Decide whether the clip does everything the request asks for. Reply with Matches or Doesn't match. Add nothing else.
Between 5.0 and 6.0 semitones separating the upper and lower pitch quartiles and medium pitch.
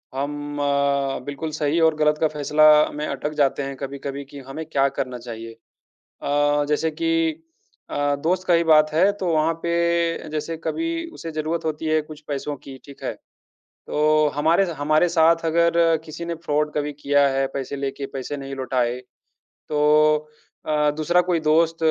Doesn't match